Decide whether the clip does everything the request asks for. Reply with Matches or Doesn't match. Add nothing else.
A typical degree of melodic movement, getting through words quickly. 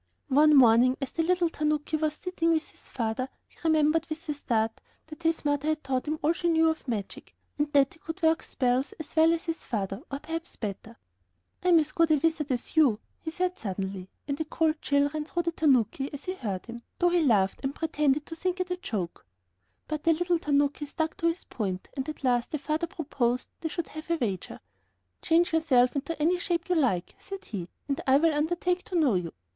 Matches